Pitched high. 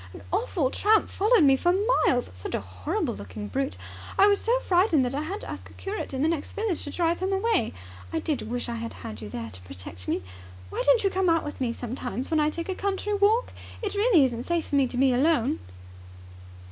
Yes: very high, 300 Hz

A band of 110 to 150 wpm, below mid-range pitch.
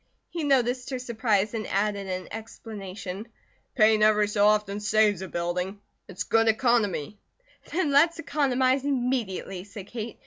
No: average, 140 wpm; high, 215 Hz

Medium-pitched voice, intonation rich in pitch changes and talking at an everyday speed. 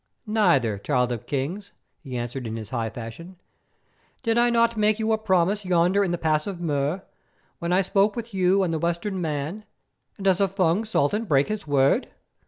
Yes: medium, 175 Hz; wide, 6.3 semitones; average, 190 wpm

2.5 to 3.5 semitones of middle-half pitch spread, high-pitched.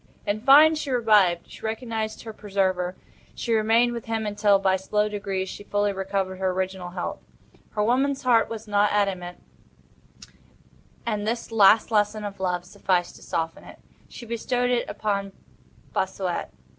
Yes: average, 2.9 semitones; high, 205 Hz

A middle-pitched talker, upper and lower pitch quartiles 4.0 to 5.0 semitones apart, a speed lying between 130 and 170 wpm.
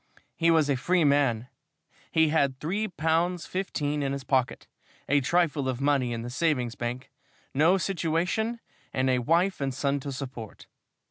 Yes: medium, 145 Hz; average, 4.3 semitones; average, 160 wpm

